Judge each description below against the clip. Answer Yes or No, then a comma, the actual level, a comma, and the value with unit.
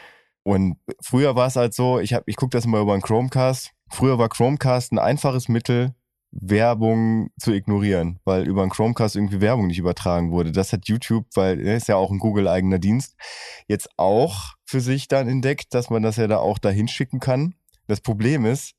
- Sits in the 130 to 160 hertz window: No, low, 115 Hz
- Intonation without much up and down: No, average, 3.7 semitones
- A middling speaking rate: No, fast, 200 wpm